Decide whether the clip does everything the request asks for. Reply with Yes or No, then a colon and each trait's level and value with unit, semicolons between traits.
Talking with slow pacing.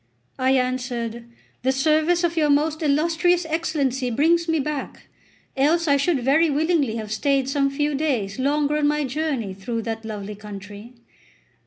No: average, 155 wpm